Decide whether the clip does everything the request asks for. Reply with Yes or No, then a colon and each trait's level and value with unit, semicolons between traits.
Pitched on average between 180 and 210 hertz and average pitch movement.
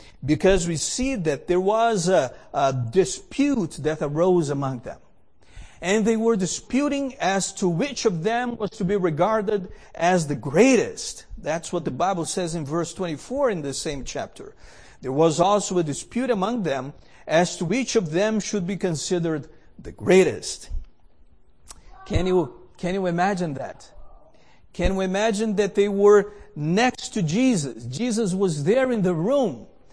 Yes: medium, 185 Hz; average, 5.0 semitones